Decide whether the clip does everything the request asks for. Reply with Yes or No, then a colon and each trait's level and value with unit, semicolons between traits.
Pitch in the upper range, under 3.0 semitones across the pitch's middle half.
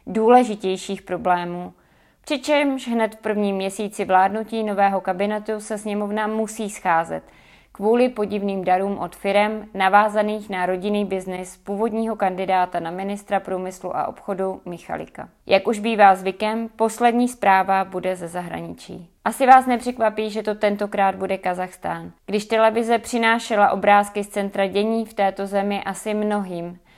Yes: high, 200 Hz; narrow, 2.5 semitones